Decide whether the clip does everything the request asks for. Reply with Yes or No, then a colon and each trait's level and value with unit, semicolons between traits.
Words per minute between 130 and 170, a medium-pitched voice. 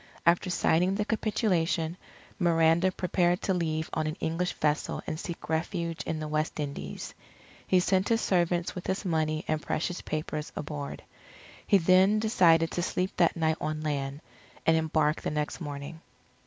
Yes: average, 160 wpm; medium, 165 Hz